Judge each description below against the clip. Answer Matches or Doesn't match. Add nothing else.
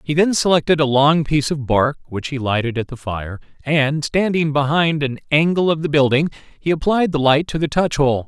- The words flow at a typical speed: Doesn't match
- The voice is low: Doesn't match